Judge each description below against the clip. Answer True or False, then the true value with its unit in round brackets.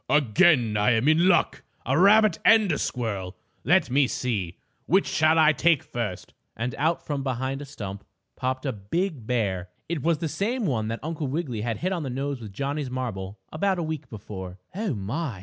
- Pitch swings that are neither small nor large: False (6.5 semitones)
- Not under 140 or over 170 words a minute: False (195 wpm)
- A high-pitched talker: False (135 Hz)